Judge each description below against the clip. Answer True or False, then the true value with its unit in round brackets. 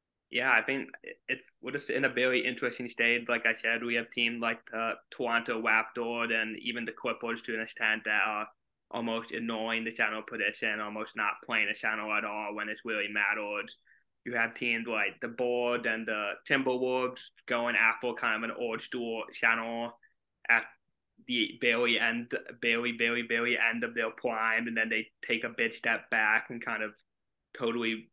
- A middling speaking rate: True (185 wpm)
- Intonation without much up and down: True (1.3 semitones)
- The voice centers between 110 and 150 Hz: True (115 Hz)